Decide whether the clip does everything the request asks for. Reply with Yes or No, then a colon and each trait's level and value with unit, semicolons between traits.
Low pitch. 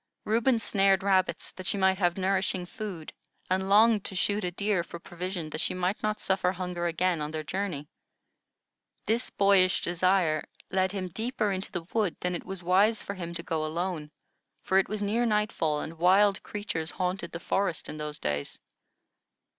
No: medium, 185 Hz